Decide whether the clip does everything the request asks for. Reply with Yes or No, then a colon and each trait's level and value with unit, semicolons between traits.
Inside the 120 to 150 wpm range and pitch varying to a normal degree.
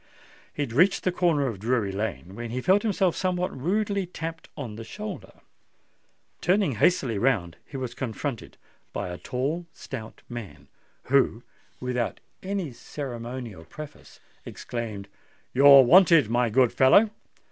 No: slow, 135 wpm; wide, 6.9 semitones